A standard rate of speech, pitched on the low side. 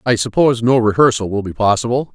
Yes: average, 195 wpm; low, 115 Hz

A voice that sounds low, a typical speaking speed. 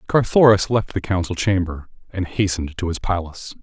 Yes: very low, 95 Hz; average, 165 wpm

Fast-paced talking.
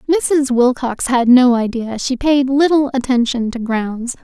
No: average, 155 wpm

